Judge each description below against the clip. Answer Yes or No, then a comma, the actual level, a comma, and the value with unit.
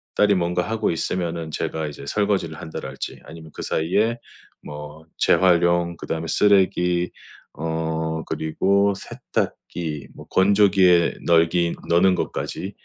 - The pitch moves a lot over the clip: No, average, 2.8 semitones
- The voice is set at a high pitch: No, very low, 85 Hz